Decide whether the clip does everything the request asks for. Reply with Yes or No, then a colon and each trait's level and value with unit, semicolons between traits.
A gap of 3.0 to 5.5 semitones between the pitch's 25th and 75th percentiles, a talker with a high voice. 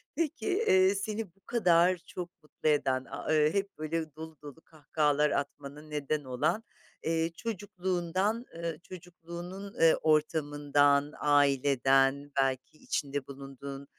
No: average, 3.8 semitones; medium, 155 Hz